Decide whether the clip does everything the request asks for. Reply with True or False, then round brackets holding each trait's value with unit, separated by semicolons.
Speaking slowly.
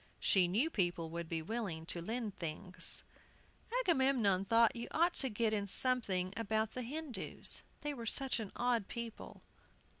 False (155 wpm)